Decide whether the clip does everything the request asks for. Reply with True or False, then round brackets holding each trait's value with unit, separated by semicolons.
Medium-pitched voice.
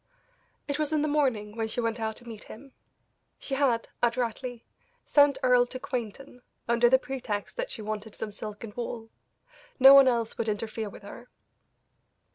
False (235 Hz)